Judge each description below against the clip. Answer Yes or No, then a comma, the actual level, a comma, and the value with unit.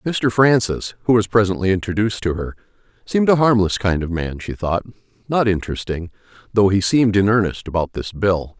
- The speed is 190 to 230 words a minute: No, average, 180 wpm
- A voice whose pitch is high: No, low, 100 Hz